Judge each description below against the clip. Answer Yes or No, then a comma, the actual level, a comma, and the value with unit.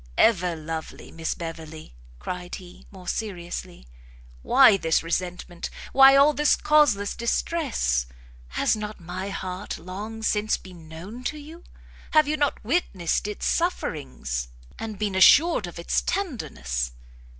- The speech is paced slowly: Yes, slow, 130 wpm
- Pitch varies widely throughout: Yes, wide, 6.6 semitones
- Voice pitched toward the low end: No, high, 190 Hz